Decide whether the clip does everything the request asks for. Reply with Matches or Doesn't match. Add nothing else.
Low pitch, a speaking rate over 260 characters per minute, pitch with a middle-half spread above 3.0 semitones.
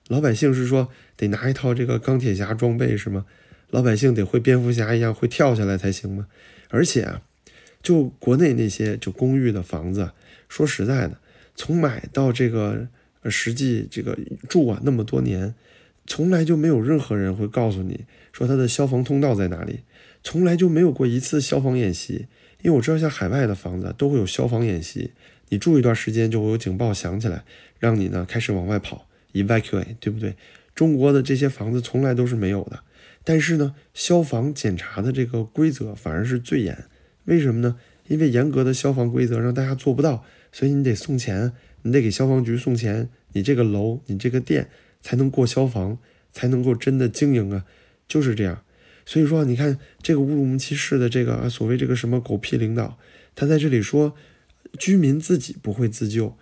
Matches